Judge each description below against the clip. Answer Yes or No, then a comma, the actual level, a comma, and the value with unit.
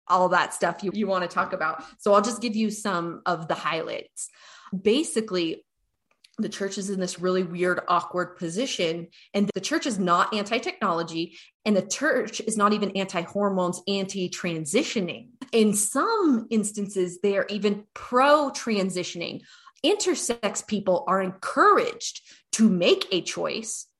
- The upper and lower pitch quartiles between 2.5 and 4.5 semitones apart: Yes, average, 3.9 semitones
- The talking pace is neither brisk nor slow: Yes, average, 155 wpm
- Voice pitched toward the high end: Yes, high, 200 Hz